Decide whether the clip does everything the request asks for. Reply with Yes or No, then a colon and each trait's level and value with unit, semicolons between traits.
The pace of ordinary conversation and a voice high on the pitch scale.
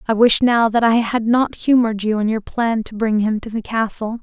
No: fast, 255 wpm; high, 225 Hz